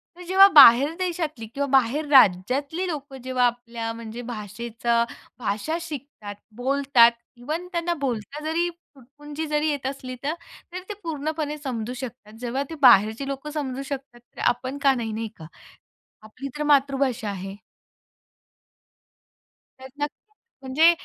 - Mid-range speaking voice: No, very high, 270 Hz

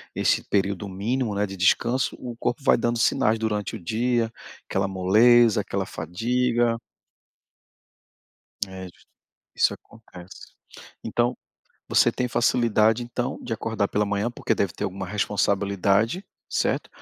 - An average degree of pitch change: Yes, average, 3.3 semitones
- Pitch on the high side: No, low, 110 Hz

